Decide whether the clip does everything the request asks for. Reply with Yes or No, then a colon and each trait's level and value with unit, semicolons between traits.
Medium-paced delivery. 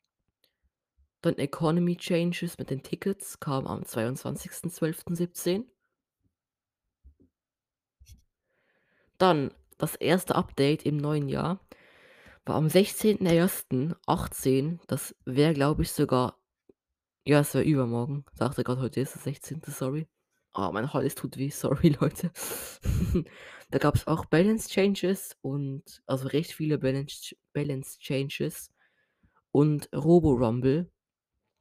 No: slow, 115 wpm